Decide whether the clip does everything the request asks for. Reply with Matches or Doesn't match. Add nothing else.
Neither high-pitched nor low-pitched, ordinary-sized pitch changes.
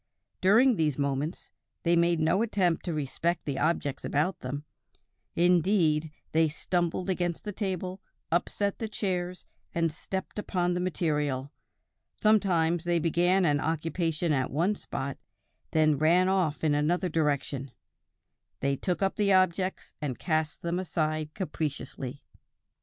Matches